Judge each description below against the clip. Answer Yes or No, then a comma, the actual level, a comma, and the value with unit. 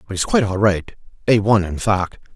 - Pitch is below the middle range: Yes, low, 100 Hz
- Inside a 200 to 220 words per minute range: Yes, fast, 205 wpm